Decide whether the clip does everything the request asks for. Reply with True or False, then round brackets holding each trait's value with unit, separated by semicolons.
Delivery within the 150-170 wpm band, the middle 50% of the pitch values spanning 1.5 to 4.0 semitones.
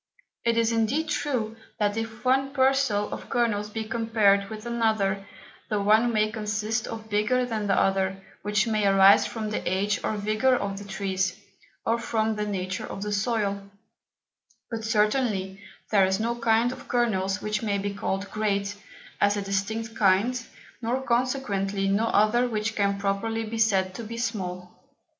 True (165 wpm; 2.5 semitones)